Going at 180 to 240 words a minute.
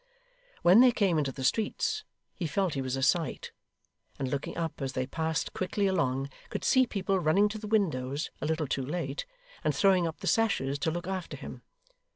Yes: average, 195 wpm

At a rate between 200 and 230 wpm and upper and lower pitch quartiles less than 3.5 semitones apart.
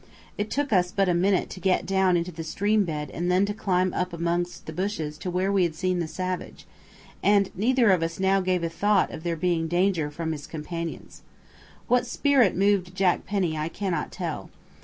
Yes: fast, 205 wpm; average, 2.8 semitones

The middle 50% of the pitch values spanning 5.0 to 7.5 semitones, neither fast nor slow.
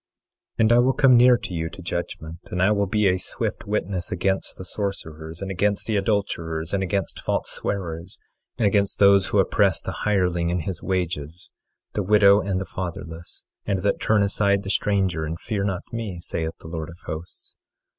No: average, 3.0 semitones; average, 195 wpm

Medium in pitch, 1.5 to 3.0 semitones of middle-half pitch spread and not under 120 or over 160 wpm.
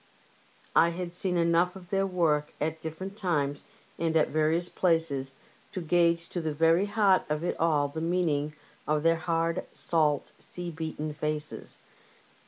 Yes: medium, 165 Hz; narrow, 2.4 semitones; average, 155 wpm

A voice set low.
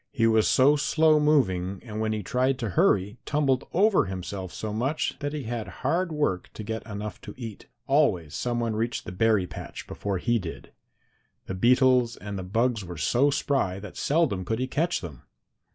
Yes: low, 115 Hz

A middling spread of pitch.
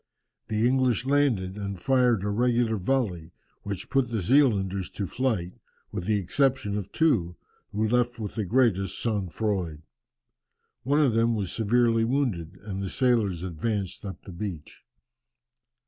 Yes: average, 4.4 semitones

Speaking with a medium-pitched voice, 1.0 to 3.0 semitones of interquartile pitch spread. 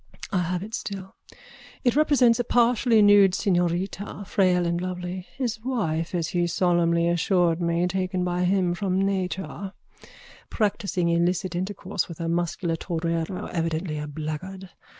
Yes: medium, 180 Hz; narrow, 2.5 semitones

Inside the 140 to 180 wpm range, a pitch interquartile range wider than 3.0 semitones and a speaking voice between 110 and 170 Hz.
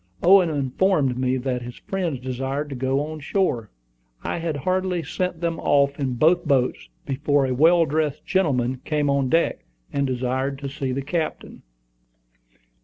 Yes: average, 160 wpm; average, 3.9 semitones; medium, 140 Hz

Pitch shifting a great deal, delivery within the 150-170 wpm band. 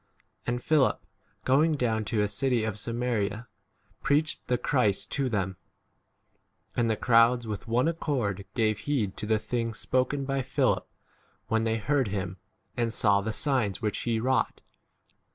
No: average, 3.4 semitones; average, 160 wpm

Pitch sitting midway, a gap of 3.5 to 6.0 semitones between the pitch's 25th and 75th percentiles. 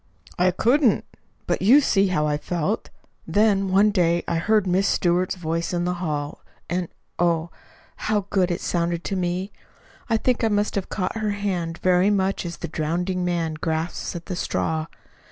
No: medium, 180 Hz; average, 2.9 semitones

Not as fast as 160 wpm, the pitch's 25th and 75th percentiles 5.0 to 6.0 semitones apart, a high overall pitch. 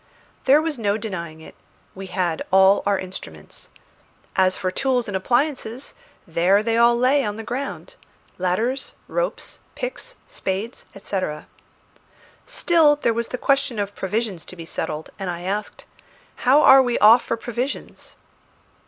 Yes: average, 145 wpm; wide, 5.5 semitones; high, 220 Hz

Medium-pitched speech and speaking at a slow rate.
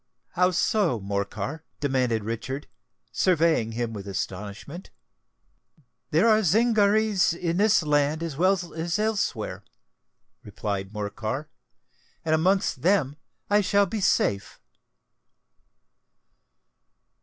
Yes: medium, 160 Hz; slow, 100 wpm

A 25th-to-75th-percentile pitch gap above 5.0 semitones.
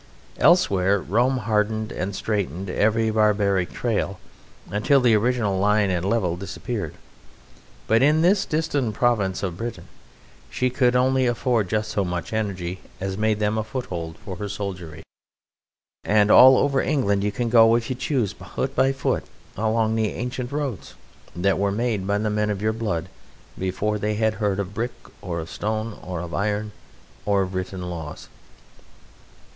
No: average, 3.4 semitones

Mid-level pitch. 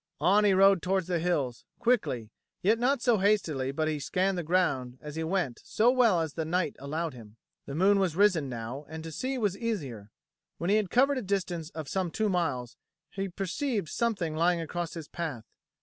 Yes: medium, 175 Hz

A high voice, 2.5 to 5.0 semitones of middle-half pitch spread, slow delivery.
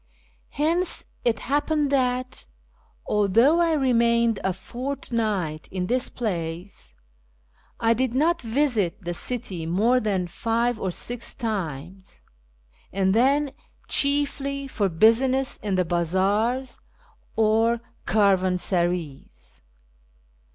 No: high, 225 Hz; wide, 5.6 semitones; slow, 100 wpm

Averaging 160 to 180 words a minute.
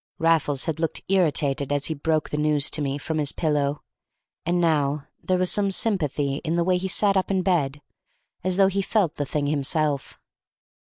No: average, 195 wpm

